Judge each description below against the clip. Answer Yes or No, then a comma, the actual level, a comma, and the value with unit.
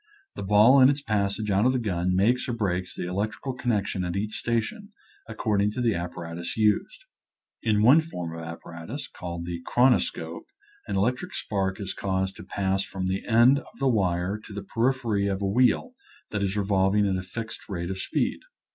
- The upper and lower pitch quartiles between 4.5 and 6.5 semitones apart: No, average, 4.0 semitones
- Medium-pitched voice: No, low, 100 Hz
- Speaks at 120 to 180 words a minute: No, average, 195 wpm